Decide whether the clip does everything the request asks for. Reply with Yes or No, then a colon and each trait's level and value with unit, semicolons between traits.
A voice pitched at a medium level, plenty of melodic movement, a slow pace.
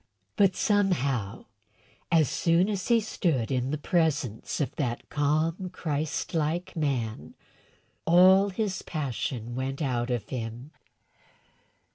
Yes: medium, 150 Hz; wide, 5.9 semitones; slow, 115 wpm